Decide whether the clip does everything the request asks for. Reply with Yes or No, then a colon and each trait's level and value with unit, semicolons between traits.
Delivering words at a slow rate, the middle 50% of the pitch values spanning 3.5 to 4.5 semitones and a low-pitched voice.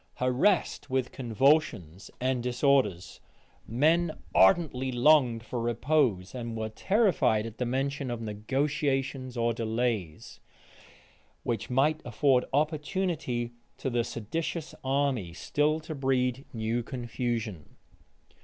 Yes: slow, 105 wpm; average, 3.8 semitones; low, 125 Hz